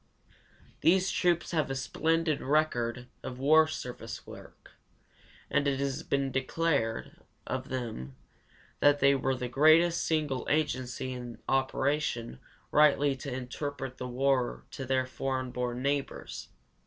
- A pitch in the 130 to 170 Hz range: Yes, low, 135 Hz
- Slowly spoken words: Yes, slow, 130 wpm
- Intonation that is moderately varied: Yes, average, 3.0 semitones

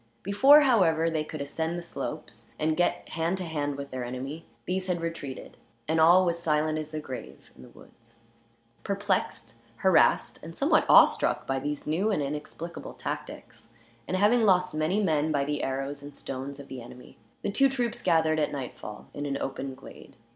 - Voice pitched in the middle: Yes, medium, 155 Hz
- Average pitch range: Yes, average, 4.1 semitones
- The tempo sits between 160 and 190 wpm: Yes, average, 185 wpm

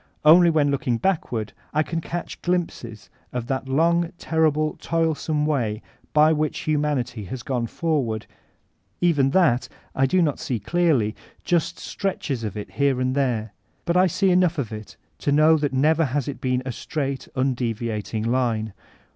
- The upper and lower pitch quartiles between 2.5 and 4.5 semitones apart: No, average, 5.0 semitones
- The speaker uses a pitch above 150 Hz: No, medium, 140 Hz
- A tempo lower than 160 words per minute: No, average, 165 wpm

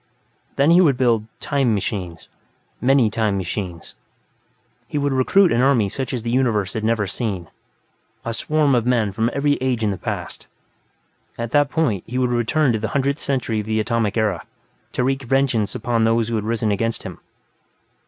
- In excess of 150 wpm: Yes, average, 185 wpm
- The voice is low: Yes, low, 115 Hz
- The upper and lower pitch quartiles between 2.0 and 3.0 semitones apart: No, average, 3.7 semitones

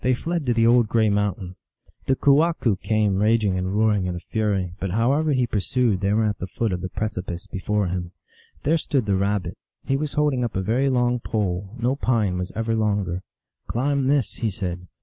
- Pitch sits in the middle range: No, low, 110 Hz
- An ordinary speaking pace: No, fast, 210 wpm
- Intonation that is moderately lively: Yes, average, 4.5 semitones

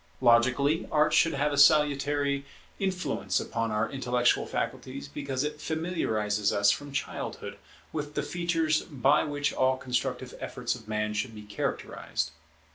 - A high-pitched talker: No, medium, 140 Hz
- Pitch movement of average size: Yes, average, 4.1 semitones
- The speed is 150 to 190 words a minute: No, average, 140 wpm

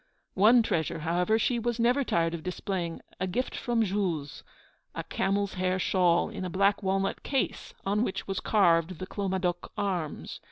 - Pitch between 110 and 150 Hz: No, high, 190 Hz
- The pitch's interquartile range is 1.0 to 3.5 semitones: Yes, average, 3.1 semitones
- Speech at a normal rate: Yes, average, 165 wpm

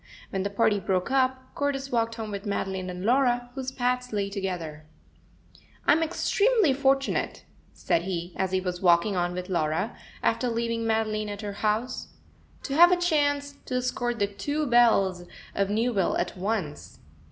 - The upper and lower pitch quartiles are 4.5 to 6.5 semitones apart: Yes, average, 5.3 semitones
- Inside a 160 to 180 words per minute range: Yes, average, 165 wpm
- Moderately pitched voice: No, high, 220 Hz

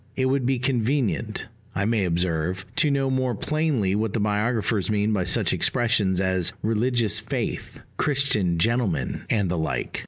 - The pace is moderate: Yes, average, 155 wpm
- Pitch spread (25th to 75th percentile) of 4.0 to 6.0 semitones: Yes, average, 5.2 semitones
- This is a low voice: Yes, low, 110 Hz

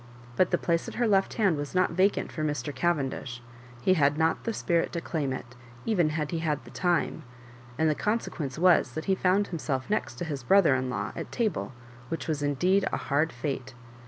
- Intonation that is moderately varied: Yes, average, 4.5 semitones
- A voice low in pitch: No, medium, 160 Hz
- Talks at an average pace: No, fast, 215 wpm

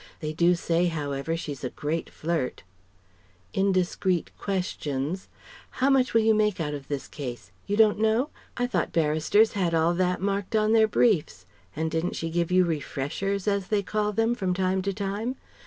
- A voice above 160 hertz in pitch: Yes, medium, 185 Hz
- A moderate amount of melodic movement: Yes, average, 4.4 semitones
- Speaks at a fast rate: No, average, 175 wpm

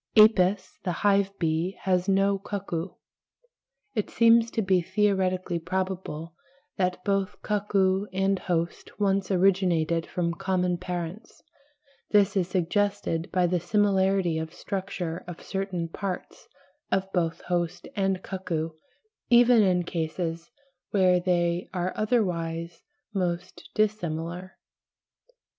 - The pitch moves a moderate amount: No, narrow, 2.3 semitones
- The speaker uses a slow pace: Yes, slow, 115 wpm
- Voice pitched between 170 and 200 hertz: Yes, medium, 185 Hz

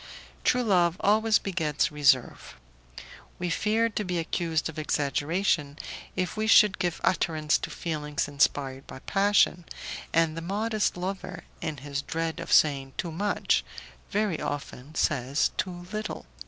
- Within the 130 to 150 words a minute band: Yes, average, 140 wpm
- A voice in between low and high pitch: Yes, medium, 165 Hz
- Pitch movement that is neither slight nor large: Yes, average, 5.0 semitones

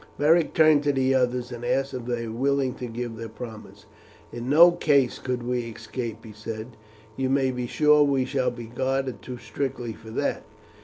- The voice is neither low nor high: No, low, 125 Hz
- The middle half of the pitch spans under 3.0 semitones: Yes, narrow, 2.5 semitones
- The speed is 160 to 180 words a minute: No, average, 195 wpm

